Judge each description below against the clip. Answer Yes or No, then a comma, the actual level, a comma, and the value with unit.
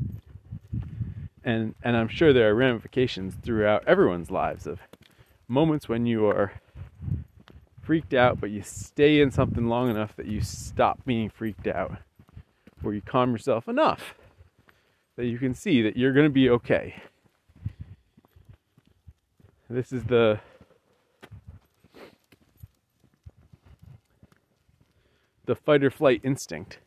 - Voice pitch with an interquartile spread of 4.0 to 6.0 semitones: No, average, 3.3 semitones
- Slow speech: Yes, slow, 120 wpm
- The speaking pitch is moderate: No, low, 115 Hz